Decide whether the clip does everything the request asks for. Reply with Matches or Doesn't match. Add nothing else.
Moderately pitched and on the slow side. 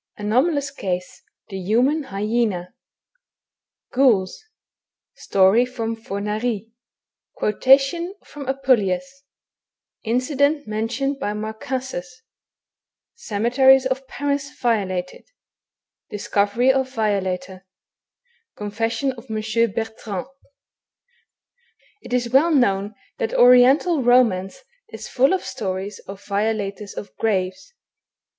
Doesn't match